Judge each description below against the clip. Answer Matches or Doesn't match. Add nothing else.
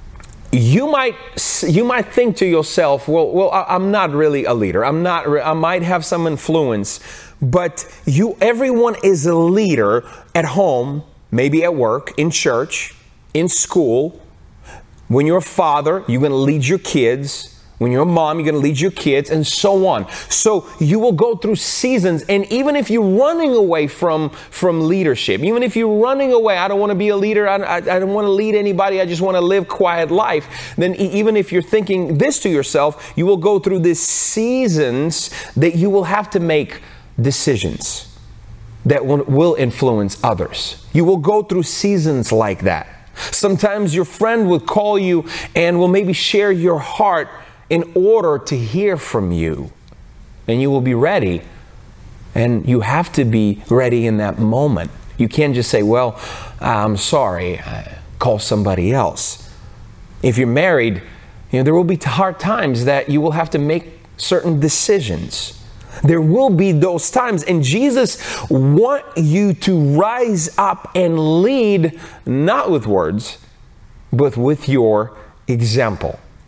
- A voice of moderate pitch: Matches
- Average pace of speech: Matches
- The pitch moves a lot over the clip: Matches